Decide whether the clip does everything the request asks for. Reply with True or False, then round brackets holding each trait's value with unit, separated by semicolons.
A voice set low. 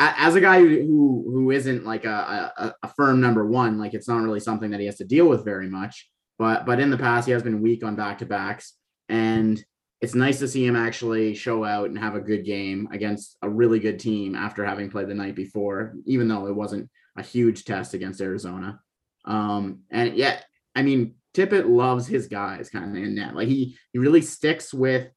True (110 Hz)